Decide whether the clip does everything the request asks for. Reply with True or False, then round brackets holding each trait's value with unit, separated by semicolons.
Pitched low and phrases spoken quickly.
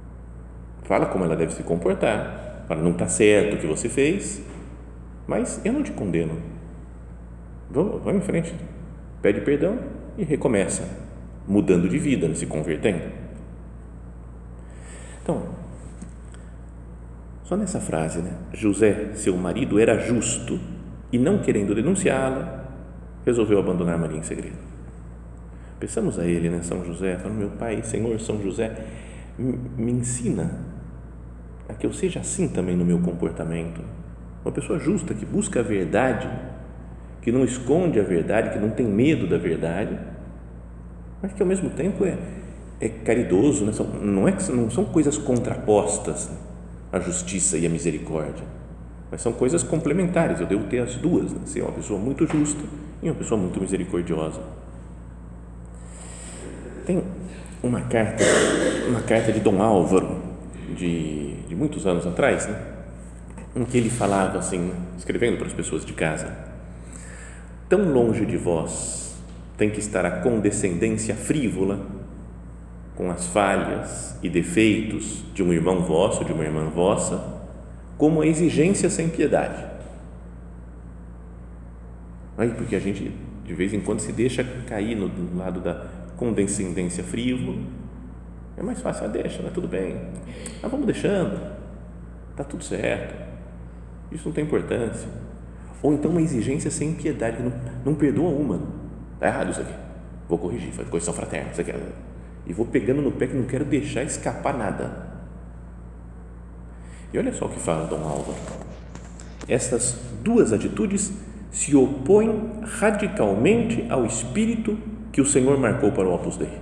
False (85 Hz; 145 wpm)